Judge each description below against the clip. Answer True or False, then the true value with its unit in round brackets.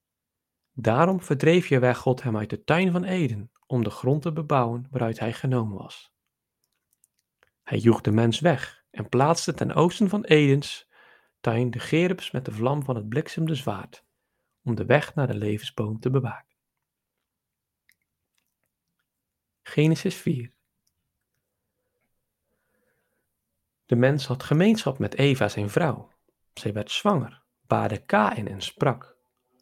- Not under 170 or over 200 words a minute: False (135 wpm)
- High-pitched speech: False (130 Hz)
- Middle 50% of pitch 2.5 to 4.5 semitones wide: False (5.2 semitones)